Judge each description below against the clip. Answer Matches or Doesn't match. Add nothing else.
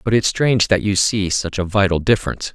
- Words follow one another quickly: Matches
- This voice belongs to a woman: Doesn't match